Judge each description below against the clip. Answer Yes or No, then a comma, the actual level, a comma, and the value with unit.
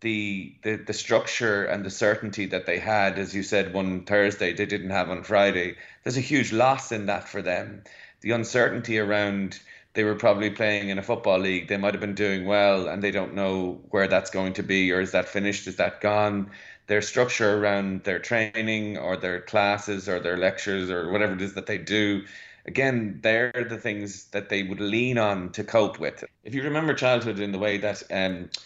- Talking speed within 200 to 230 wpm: Yes, fast, 205 wpm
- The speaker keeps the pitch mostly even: Yes, narrow, 1.9 semitones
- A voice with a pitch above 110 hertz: No, low, 100 Hz